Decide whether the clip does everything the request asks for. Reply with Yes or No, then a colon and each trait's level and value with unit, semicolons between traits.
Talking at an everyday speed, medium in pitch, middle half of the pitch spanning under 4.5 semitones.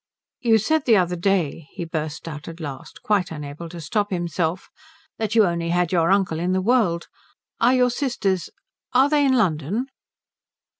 No: average, 170 wpm; medium, 180 Hz; average, 5.1 semitones